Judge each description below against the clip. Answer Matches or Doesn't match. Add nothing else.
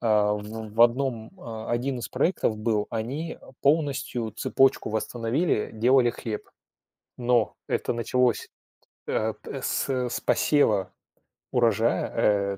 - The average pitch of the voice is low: Matches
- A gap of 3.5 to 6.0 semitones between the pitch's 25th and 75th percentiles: Doesn't match